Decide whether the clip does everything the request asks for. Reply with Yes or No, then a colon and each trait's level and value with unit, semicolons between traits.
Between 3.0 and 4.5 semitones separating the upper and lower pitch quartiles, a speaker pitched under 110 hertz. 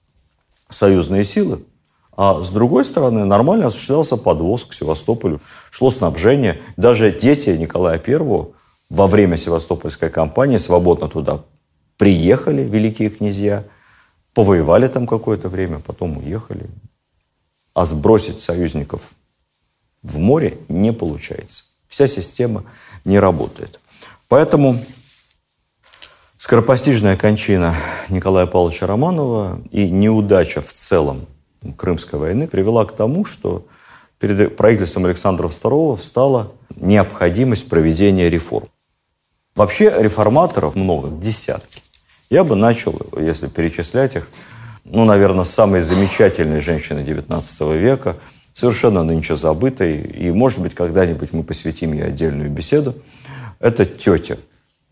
No: average, 5.1 semitones; low, 100 Hz